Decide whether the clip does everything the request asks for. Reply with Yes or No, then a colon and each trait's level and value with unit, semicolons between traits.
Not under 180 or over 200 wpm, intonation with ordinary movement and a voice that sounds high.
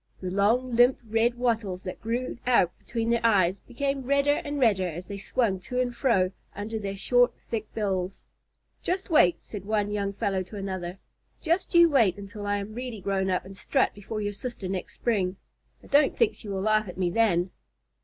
Yes: average, 195 wpm; average, 4.2 semitones; high, 210 Hz